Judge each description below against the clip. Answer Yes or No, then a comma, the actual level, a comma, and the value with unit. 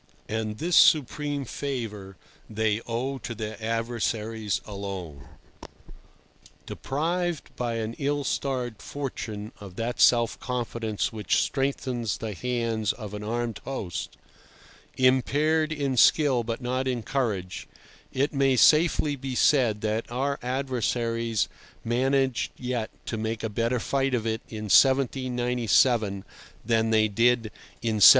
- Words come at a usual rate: No, slow, 125 wpm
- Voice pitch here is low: Yes, low, 120 Hz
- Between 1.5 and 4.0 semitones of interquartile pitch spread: Yes, average, 3.4 semitones